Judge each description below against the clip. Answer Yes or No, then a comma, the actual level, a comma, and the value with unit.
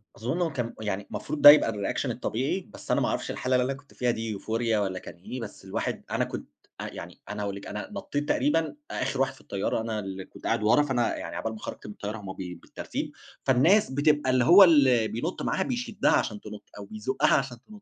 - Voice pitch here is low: Yes, low, 120 Hz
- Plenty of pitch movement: Yes, wide, 5.7 semitones